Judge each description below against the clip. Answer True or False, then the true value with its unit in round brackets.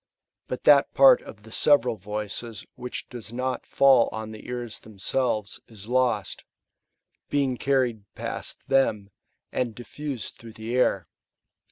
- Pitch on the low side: True (120 Hz)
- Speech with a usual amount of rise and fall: True (3.0 semitones)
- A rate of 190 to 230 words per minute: False (140 wpm)